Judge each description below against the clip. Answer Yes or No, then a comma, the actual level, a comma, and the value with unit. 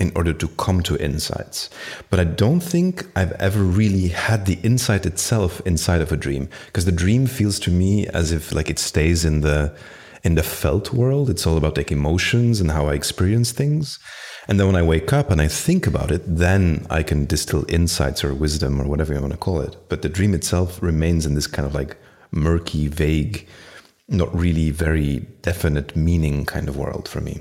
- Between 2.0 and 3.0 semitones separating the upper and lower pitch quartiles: No, average, 4.3 semitones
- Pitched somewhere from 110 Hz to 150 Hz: No, very low, 85 Hz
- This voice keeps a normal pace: No, fast, 210 wpm